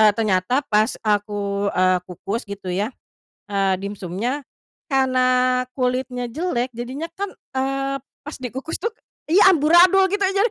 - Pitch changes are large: Yes, wide, 5.7 semitones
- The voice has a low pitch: No, very high, 250 Hz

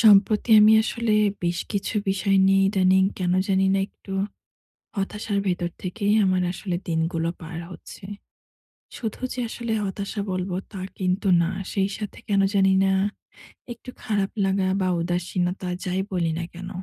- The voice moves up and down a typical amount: No, narrow, 1.9 semitones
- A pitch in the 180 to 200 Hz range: Yes, high, 190 Hz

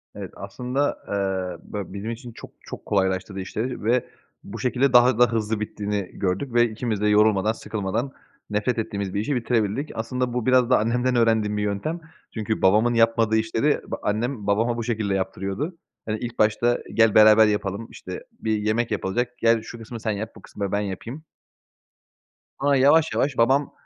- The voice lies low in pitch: Yes, low, 110 Hz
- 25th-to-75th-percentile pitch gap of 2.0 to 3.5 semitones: Yes, average, 2.9 semitones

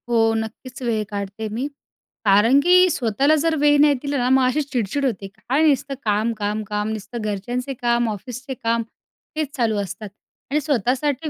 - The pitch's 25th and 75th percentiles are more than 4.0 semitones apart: Yes, average, 4.6 semitones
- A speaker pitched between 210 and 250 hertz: Yes, high, 240 Hz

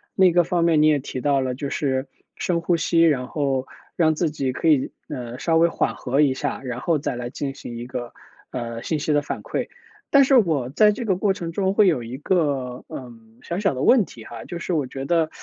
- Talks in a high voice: No, medium, 150 Hz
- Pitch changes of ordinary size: Yes, average, 4.8 semitones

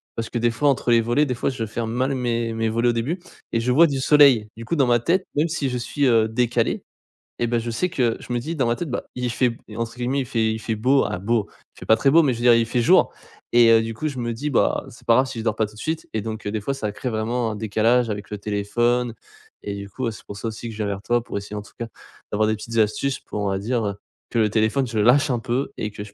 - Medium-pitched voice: No, low, 115 Hz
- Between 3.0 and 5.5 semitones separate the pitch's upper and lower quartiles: No, narrow, 2.4 semitones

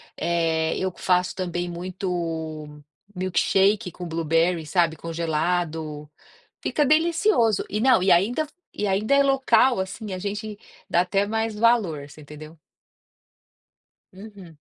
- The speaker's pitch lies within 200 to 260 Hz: No, medium, 185 Hz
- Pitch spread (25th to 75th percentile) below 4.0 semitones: No, average, 4.7 semitones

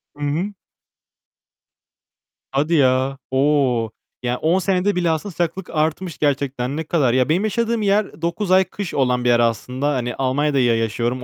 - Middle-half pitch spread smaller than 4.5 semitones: No, wide, 5.6 semitones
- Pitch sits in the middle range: Yes, medium, 145 Hz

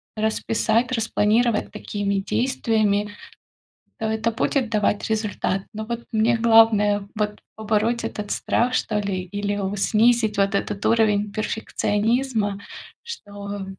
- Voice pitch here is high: Yes, high, 215 Hz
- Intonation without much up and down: Yes, narrow, 1.8 semitones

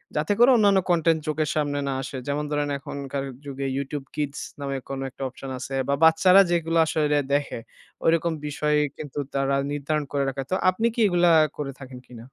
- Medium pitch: Yes, medium, 145 Hz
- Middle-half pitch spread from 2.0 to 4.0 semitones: Yes, average, 2.9 semitones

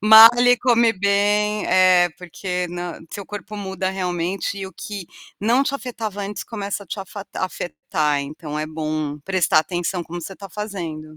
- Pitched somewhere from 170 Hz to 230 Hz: Yes, high, 190 Hz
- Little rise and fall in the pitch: No, average, 3.2 semitones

